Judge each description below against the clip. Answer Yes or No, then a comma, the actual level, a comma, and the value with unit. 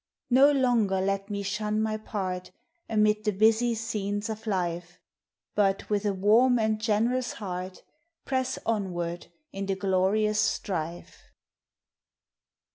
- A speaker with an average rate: No, slow, 120 wpm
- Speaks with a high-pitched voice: Yes, high, 210 Hz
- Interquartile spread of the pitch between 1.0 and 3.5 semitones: Yes, narrow, 2.4 semitones